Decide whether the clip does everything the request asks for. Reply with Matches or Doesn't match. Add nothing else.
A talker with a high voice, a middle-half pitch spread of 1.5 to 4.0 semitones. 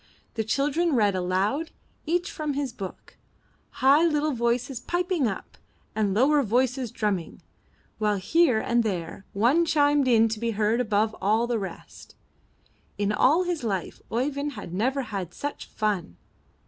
Doesn't match